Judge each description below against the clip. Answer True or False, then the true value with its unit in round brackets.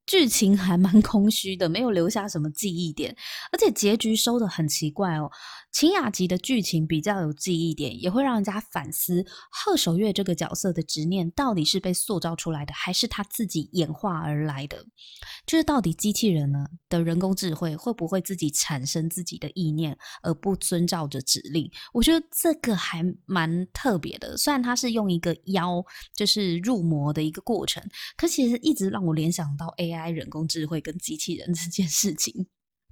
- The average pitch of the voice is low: False (180 Hz)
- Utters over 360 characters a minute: False (285 characters per minute)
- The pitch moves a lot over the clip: False (4.7 semitones)